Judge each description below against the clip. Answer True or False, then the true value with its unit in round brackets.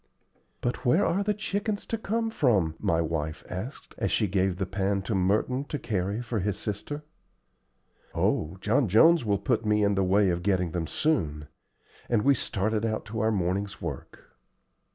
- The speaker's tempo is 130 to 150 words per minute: False (175 wpm)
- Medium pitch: False (105 Hz)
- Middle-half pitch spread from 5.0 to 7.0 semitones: True (5.3 semitones)